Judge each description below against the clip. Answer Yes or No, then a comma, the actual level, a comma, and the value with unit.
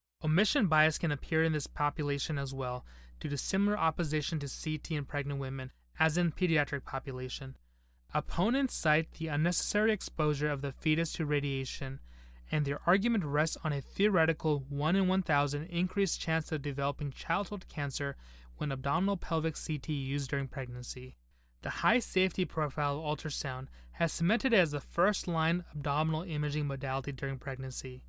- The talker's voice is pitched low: No, medium, 150 Hz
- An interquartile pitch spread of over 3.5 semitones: No, average, 3.2 semitones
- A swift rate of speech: No, average, 160 wpm